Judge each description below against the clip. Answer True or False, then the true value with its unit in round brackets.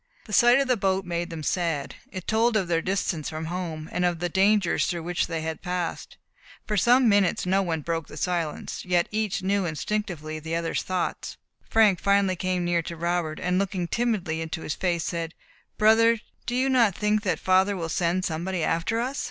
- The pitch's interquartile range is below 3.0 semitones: False (3.5 semitones)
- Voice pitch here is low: False (180 Hz)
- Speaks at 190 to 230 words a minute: True (200 wpm)